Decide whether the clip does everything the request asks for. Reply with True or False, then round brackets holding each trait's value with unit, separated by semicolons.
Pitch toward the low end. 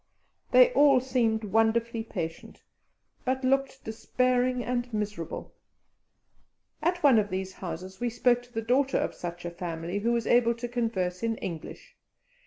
False (230 Hz)